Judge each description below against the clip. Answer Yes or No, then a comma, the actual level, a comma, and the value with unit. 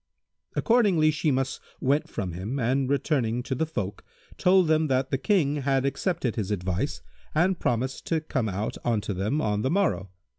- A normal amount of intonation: No, wide, 6.0 semitones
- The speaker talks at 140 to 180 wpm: Yes, average, 170 wpm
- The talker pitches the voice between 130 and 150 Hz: Yes, low, 135 Hz